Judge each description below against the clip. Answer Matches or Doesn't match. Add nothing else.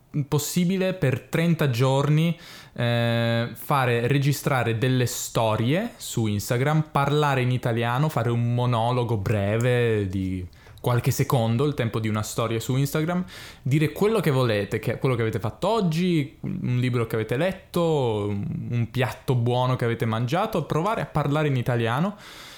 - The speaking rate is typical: Matches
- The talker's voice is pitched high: Doesn't match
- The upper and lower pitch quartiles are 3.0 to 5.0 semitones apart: Matches